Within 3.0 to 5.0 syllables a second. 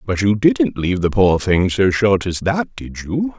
Yes: 4.3 syllables/s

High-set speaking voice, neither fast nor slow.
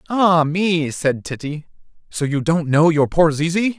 No: medium, 165 Hz; average, 175 wpm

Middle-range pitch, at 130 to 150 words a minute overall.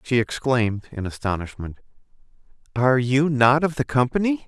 No: low, 130 Hz; slow, 135 wpm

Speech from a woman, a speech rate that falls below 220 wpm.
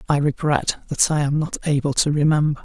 No: male; fast, 205 wpm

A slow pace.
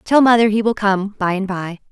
No: fast, 250 wpm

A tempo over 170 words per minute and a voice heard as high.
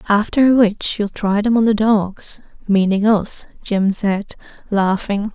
No: slow, 135 wpm; high, 205 Hz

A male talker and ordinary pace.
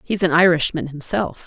No: female; average, 165 wpm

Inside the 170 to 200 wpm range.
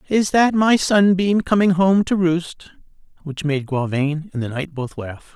Yes: average, 180 wpm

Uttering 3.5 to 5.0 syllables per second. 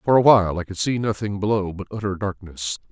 No: 6.1 syllables/s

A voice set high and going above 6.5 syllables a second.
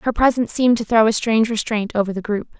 Yes: high, 220 Hz; 6.8 syllables/s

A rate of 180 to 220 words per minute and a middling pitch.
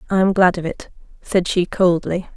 Yes: fast, 205 wpm; medium, 180 Hz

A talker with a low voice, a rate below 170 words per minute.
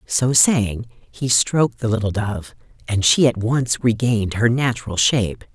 Yes: low, 115 Hz; average, 160 wpm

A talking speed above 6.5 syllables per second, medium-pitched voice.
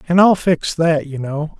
No: 4.2 syllables/s; medium, 160 Hz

